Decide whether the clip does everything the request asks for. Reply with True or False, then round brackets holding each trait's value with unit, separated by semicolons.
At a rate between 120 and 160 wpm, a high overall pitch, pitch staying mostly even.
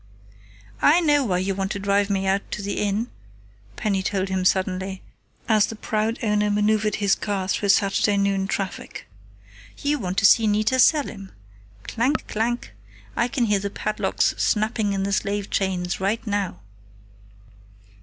True (155 wpm; 205 Hz; 1.9 semitones)